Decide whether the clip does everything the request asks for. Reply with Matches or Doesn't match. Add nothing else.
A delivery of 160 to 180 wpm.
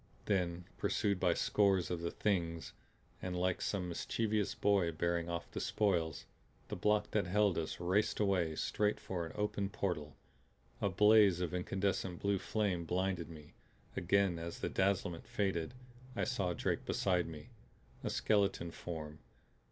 Doesn't match